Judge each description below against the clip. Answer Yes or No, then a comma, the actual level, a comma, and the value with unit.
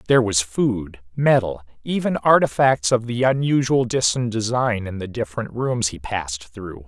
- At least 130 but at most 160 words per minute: Yes, average, 155 wpm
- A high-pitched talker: No, low, 115 Hz